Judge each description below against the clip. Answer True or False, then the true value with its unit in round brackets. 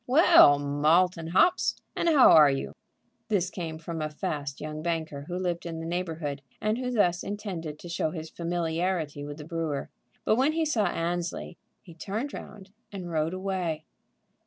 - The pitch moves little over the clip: False (3.4 semitones)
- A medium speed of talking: True (175 wpm)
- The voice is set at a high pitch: False (170 Hz)